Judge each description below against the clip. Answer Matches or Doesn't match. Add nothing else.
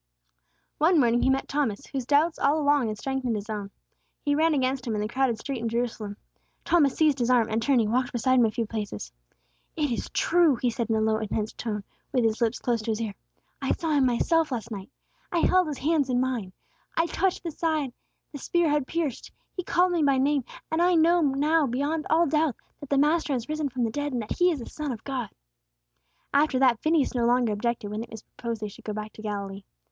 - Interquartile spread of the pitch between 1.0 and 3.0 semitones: Doesn't match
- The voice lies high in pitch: Matches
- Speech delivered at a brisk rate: Matches